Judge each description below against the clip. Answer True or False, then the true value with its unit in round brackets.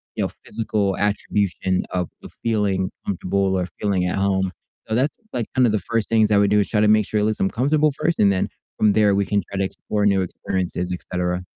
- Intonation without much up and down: True (2.2 semitones)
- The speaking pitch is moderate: False (100 Hz)